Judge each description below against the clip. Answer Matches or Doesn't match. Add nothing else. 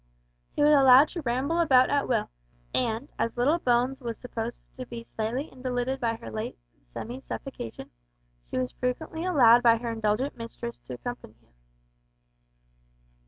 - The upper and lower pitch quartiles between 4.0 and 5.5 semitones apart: Doesn't match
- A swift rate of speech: Doesn't match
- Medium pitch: Doesn't match